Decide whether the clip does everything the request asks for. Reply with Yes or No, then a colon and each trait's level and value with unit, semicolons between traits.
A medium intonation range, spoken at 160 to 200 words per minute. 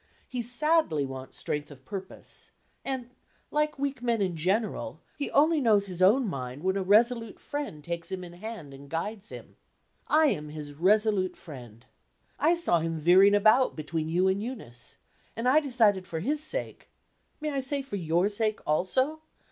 No: wide, 7.5 semitones; average, 170 wpm